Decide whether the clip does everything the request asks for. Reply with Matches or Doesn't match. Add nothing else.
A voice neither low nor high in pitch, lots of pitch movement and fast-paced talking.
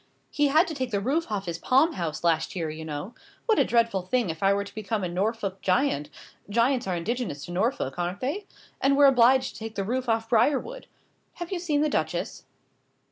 Doesn't match